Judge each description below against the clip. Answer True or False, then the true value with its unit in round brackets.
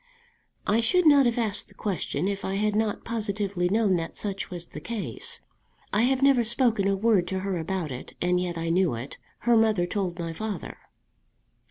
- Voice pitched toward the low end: False (200 Hz)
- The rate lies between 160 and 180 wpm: False (195 wpm)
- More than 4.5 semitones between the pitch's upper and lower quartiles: False (4.2 semitones)